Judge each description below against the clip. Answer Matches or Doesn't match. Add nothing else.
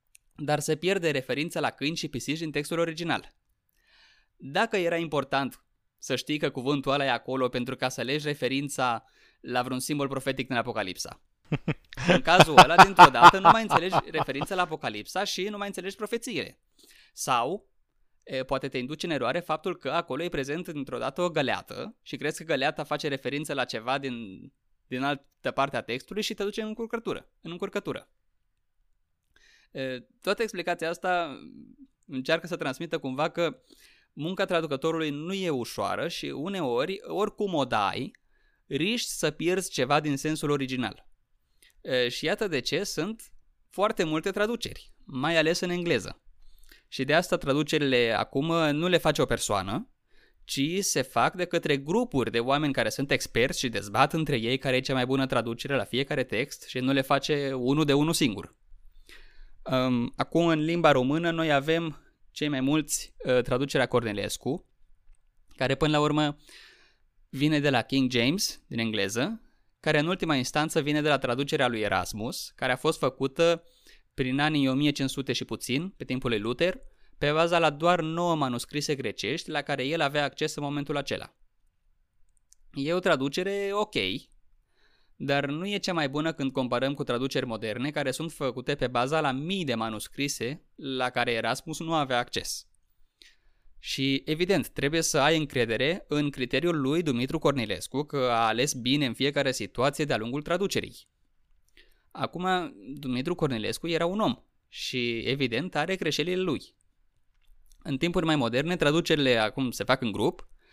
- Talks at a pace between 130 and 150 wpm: Doesn't match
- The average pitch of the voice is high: Doesn't match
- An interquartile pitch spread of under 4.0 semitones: Doesn't match